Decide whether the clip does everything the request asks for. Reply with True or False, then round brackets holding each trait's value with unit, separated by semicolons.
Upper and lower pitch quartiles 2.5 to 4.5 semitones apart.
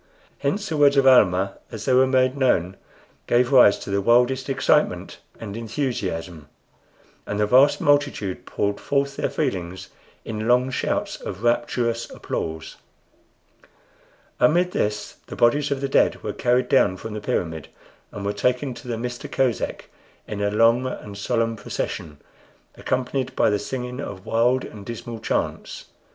True (4.2 semitones)